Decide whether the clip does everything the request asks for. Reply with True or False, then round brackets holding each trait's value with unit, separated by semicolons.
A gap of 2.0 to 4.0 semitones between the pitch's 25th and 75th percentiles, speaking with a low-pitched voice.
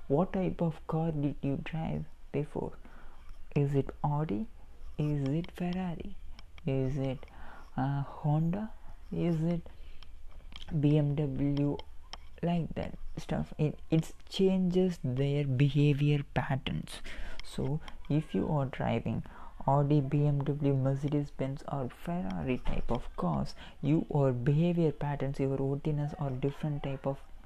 False (2.9 semitones; 145 Hz)